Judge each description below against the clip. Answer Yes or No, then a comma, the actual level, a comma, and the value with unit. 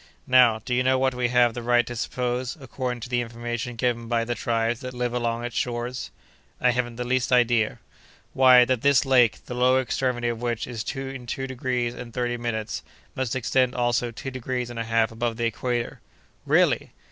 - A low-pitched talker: Yes, low, 120 Hz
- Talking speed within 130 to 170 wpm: No, average, 200 wpm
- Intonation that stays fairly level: Yes, narrow, 1.3 semitones